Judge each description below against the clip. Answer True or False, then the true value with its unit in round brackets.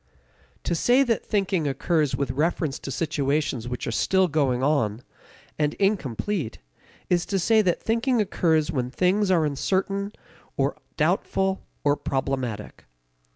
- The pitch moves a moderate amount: False (6.0 semitones)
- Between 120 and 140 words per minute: True (135 wpm)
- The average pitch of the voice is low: False (155 Hz)